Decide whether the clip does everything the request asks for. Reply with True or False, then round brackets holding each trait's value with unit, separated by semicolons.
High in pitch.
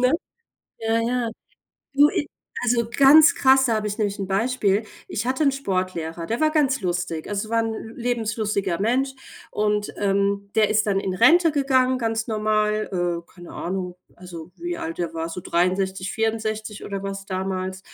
True (215 Hz)